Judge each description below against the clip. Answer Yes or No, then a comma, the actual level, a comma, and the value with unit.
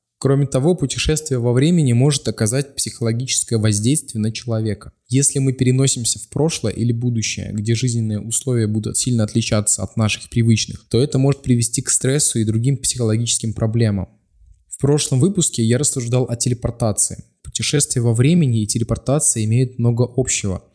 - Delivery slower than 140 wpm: No, average, 150 wpm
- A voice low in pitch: Yes, low, 120 Hz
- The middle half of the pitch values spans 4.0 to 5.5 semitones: No, average, 3.2 semitones